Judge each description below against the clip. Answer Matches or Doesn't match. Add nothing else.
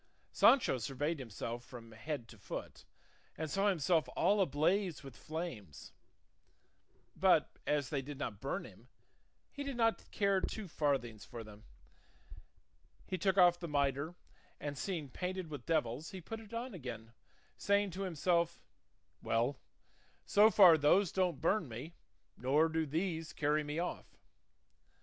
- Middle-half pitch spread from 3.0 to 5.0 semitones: Doesn't match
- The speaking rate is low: Doesn't match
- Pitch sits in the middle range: Matches